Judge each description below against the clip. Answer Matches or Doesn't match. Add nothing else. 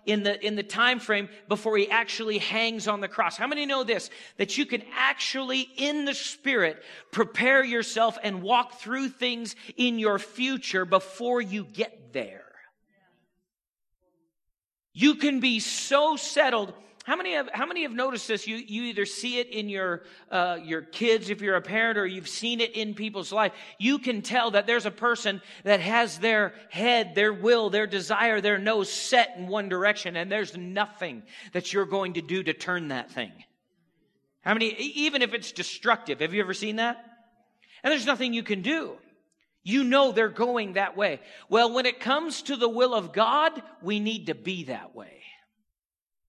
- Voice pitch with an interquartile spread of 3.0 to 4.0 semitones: Matches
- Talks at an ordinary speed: Matches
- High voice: Matches